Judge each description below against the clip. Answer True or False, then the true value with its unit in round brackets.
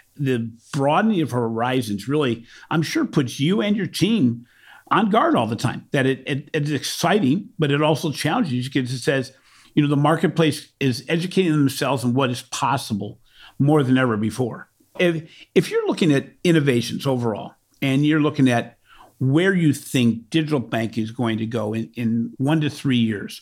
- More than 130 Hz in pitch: True (140 Hz)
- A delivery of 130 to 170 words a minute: False (180 wpm)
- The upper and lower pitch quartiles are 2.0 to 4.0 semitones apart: False (4.4 semitones)